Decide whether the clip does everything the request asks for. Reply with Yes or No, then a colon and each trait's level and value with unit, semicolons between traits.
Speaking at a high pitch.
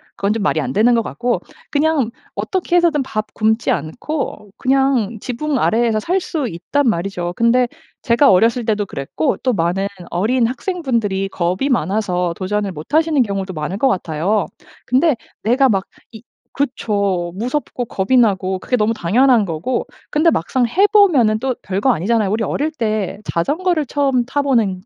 Yes: high, 225 Hz